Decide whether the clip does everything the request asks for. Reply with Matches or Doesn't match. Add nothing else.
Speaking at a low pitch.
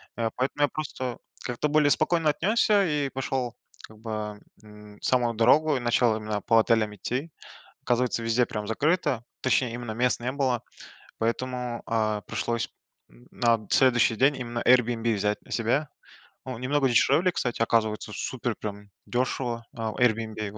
Matches